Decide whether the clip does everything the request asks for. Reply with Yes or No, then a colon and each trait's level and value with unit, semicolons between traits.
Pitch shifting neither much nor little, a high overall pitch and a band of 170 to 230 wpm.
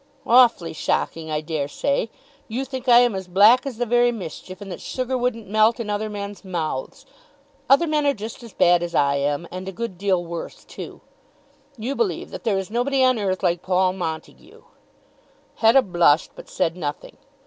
No: wide, 5.7 semitones; high, 205 Hz; average, 190 wpm